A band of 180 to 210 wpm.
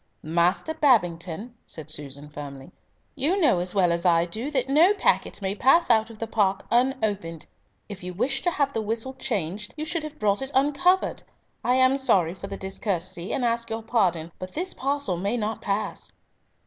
Yes: average, 185 wpm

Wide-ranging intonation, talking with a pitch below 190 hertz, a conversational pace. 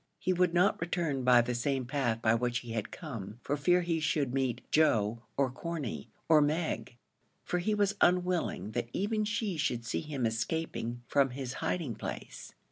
Yes: wide, 6.2 semitones; medium, 140 Hz; average, 180 wpm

